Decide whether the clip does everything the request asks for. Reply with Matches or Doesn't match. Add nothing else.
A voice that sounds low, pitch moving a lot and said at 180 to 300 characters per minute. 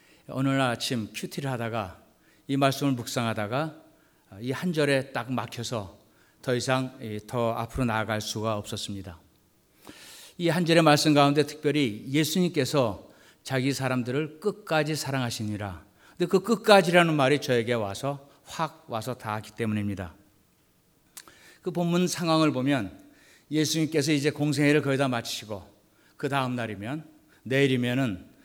Doesn't match